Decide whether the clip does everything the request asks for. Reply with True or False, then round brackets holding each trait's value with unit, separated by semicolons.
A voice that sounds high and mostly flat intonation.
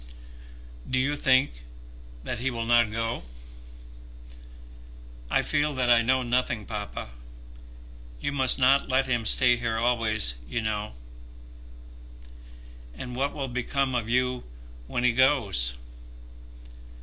False (120 Hz; 2.3 semitones)